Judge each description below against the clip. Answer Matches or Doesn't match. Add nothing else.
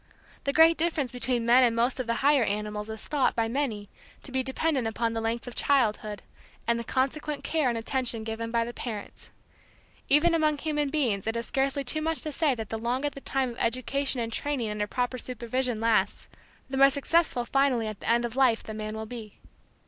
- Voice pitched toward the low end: Doesn't match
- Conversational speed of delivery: Doesn't match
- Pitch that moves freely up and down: Doesn't match